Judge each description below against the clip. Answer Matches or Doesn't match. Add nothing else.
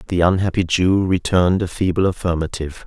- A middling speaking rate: Matches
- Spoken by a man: Matches